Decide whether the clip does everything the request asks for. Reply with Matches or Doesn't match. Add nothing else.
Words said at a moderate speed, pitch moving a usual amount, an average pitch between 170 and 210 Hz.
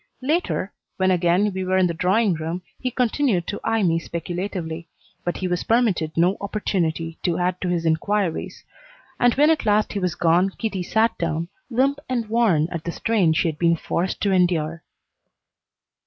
Matches